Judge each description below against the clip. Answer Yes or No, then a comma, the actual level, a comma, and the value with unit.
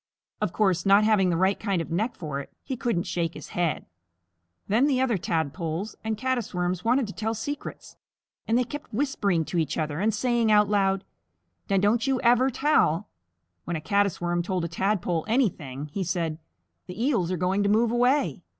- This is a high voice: Yes, high, 200 Hz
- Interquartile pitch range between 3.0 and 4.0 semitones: No, average, 5.2 semitones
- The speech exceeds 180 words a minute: Yes, average, 195 wpm